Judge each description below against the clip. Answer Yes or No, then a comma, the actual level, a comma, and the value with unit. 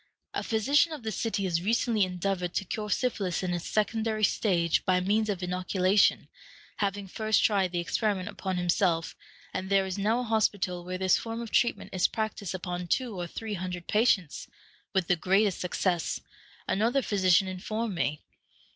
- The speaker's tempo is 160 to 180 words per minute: Yes, average, 170 wpm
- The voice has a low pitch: No, high, 195 Hz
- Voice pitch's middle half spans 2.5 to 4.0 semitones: Yes, average, 3.2 semitones